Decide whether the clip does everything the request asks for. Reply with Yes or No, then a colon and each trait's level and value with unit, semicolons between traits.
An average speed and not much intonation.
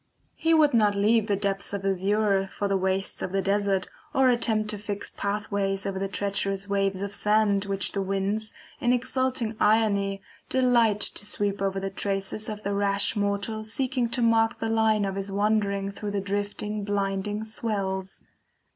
Yes: average, 175 wpm; narrow, 1.8 semitones